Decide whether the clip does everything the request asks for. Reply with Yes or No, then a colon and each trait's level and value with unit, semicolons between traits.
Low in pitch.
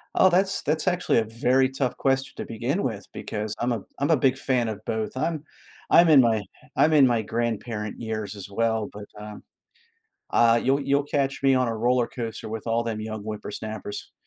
Yes: low, 120 Hz